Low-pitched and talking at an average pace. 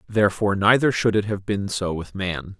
No: low, 100 Hz; fast, 210 wpm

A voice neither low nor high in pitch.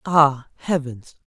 Yes: medium, 145 Hz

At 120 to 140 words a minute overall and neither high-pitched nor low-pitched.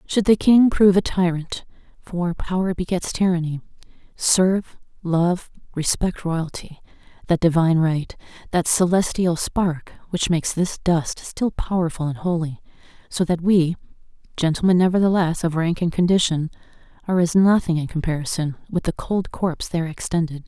Yes: slow, 135 wpm; medium, 175 Hz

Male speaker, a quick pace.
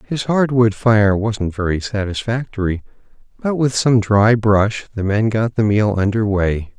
No: male; average, 170 wpm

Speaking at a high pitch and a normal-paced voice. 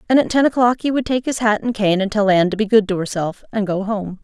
No: high, 215 Hz; fast, 310 wpm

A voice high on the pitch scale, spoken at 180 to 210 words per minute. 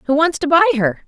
No: very high, 295 Hz; fast, 280 wpm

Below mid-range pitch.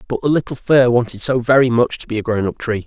Yes: low, 120 Hz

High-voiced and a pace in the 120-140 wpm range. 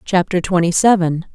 No: medium, 180 Hz; slow, 135 wpm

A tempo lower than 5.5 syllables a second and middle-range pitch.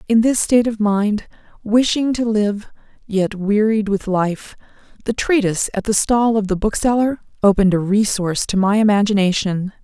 No: 5.0 syllables/s; high, 210 Hz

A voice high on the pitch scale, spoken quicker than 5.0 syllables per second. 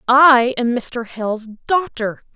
No: high, 245 Hz; 3.4 syllables/s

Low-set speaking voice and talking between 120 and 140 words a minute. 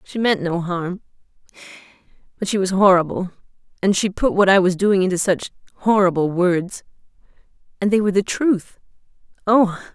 No: high, 190 Hz; slow, 135 wpm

